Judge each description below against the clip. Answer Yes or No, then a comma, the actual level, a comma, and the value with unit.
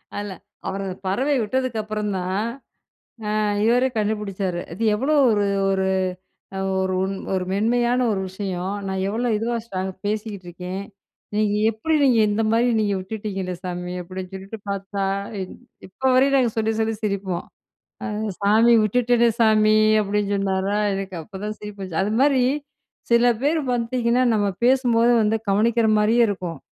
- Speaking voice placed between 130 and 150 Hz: No, high, 210 Hz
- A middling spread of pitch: Yes, average, 3.4 semitones